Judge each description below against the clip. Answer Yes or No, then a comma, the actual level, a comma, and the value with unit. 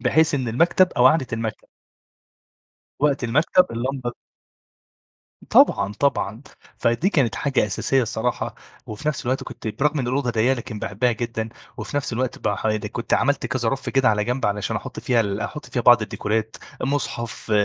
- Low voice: Yes, low, 120 Hz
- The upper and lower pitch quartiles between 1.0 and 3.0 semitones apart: No, average, 3.6 semitones